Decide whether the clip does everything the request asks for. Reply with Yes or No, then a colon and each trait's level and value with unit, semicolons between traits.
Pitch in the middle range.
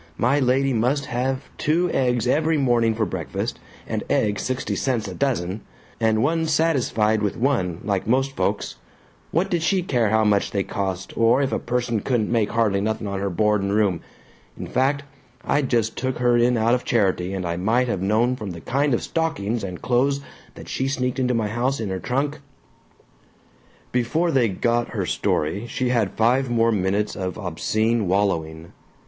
No: low, 115 Hz